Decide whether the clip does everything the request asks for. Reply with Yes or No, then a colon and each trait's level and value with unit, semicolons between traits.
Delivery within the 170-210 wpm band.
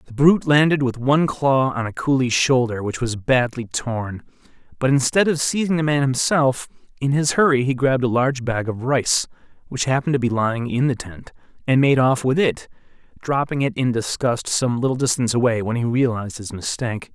Yes: average, 200 wpm